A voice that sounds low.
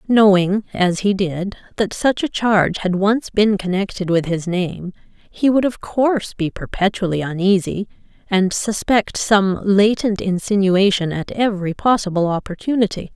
No: high, 200 Hz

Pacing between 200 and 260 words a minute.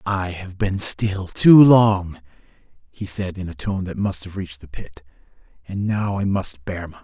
Yes: fast, 205 wpm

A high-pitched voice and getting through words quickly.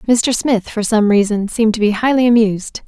Yes: high, 220 Hz; fast, 210 wpm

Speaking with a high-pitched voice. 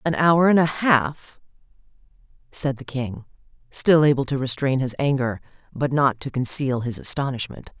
No: low, 135 Hz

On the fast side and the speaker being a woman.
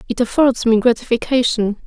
No: slow, 130 wpm; female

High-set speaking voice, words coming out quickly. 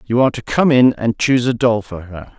No: low, 115 Hz; fast, 275 wpm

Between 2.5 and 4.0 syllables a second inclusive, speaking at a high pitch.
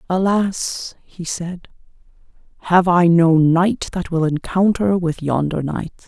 No: 3.5 syllables/s; medium, 175 Hz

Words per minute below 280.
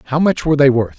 No: fast, 305 wpm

